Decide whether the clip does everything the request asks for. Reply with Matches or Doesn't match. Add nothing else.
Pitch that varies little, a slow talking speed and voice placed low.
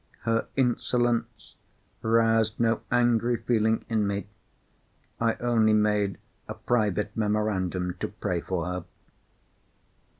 Matches